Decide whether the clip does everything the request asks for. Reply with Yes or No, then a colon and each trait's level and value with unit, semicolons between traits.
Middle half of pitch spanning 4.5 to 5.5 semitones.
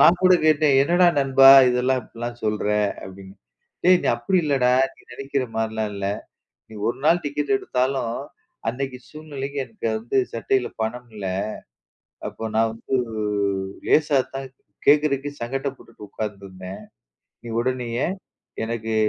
No: average, 3.9 semitones